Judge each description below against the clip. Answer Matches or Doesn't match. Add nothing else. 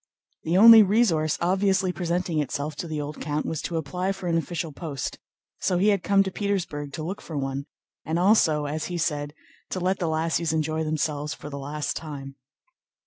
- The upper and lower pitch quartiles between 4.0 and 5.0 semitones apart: Doesn't match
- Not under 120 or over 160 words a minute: Doesn't match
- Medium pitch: Matches